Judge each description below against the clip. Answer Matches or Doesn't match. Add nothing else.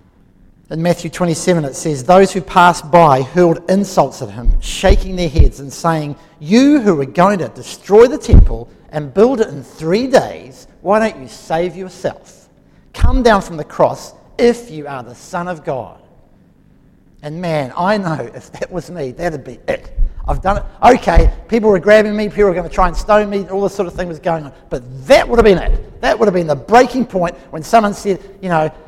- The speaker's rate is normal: Doesn't match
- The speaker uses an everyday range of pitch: Matches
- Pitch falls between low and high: Matches